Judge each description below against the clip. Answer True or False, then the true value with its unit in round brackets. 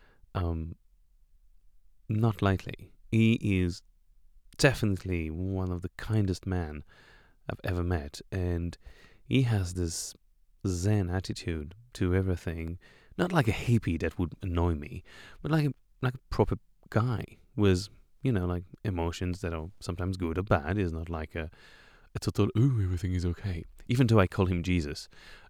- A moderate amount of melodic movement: True (3.8 semitones)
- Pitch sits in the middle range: False (90 Hz)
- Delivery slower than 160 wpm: True (150 wpm)